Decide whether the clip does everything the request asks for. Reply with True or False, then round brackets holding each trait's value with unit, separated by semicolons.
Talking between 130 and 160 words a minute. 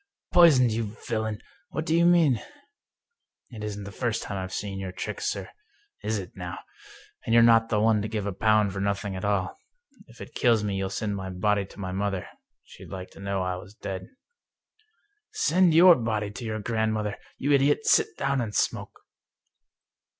False (205 wpm)